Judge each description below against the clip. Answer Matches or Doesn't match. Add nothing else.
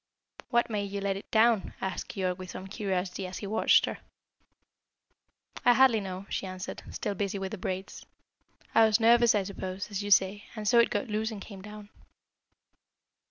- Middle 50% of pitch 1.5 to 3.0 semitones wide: Matches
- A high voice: Matches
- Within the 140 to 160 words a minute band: Doesn't match